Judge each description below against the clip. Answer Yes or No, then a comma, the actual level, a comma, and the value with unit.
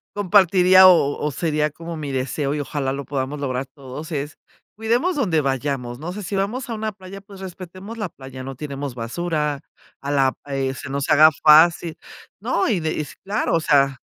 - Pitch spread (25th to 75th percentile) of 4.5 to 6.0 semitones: Yes, average, 5.3 semitones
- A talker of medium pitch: Yes, medium, 150 Hz